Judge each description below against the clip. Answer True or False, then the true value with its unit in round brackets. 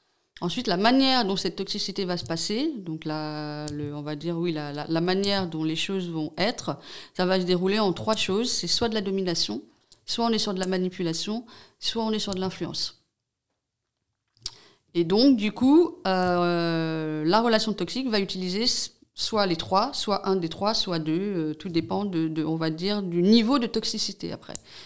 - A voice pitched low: False (185 Hz)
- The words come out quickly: False (200 wpm)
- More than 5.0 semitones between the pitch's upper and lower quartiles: False (4.7 semitones)